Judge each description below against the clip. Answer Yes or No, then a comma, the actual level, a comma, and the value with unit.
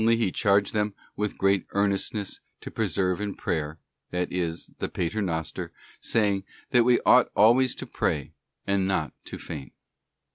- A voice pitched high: No, low, 100 Hz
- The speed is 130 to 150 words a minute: Yes, average, 140 wpm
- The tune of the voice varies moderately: Yes, average, 3.2 semitones